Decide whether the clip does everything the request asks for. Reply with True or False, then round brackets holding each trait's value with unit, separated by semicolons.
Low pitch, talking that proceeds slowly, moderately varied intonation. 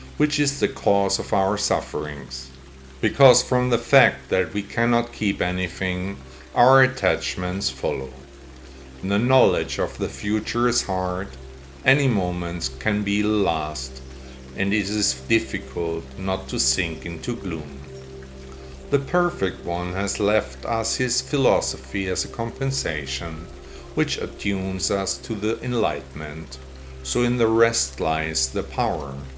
False (90 Hz; 130 wpm; 8.4 semitones)